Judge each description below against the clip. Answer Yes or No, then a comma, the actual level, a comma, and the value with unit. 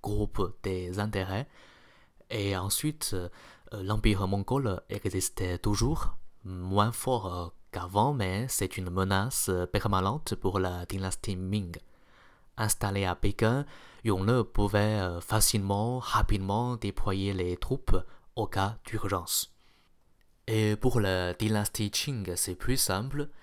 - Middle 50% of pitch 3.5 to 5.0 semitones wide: No, average, 2.7 semitones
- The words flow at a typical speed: No, slow, 105 wpm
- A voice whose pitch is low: Yes, low, 100 Hz